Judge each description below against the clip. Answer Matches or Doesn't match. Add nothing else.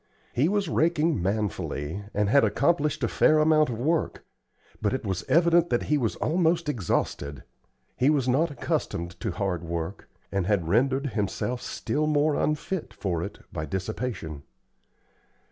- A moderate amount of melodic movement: Doesn't match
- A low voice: Matches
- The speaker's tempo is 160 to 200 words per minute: Doesn't match